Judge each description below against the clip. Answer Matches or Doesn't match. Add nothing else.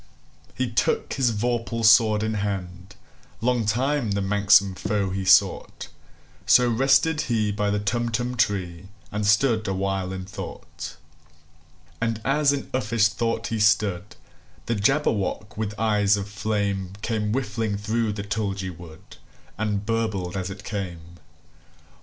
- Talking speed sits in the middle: Doesn't match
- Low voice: Matches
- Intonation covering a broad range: Doesn't match